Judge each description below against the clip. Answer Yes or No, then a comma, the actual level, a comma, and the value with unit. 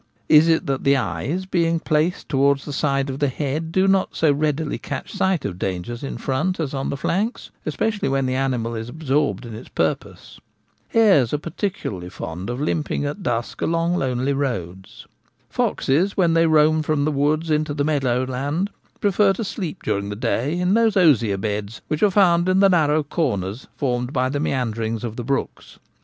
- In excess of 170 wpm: Yes, average, 190 wpm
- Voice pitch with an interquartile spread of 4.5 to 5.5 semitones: Yes, average, 5.1 semitones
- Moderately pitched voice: Yes, medium, 145 Hz